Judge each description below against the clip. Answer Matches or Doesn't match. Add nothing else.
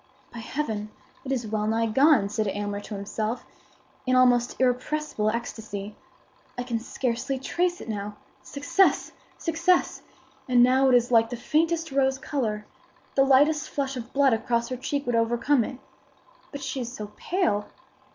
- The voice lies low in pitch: Doesn't match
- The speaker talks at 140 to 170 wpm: Matches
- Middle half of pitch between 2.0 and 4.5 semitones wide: Matches